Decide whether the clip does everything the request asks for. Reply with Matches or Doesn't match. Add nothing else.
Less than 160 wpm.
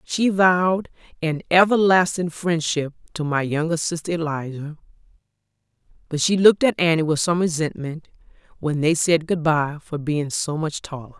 Matches